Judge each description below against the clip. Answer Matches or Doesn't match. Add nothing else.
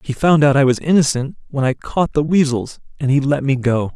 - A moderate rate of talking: Doesn't match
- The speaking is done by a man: Matches